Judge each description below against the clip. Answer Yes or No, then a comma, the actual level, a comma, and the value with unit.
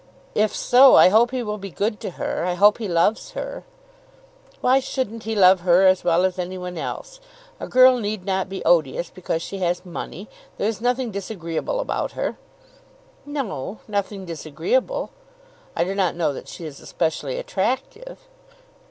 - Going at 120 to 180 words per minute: Yes, average, 170 wpm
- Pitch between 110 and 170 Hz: No, high, 195 Hz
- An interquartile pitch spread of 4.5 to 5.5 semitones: Yes, average, 4.8 semitones